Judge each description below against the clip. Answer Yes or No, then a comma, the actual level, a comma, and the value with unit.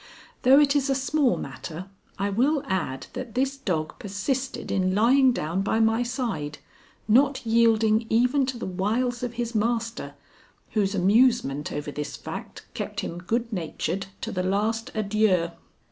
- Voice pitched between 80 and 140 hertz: No, high, 225 Hz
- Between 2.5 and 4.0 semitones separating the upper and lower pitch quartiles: No, average, 4.7 semitones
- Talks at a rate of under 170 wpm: Yes, average, 155 wpm